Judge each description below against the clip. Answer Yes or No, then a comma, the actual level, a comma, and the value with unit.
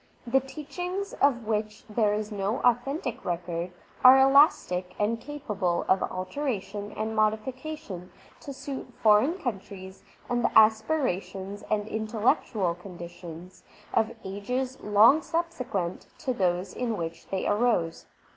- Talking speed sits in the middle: No, slow, 125 wpm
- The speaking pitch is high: Yes, high, 215 Hz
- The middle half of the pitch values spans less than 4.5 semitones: No, wide, 5.5 semitones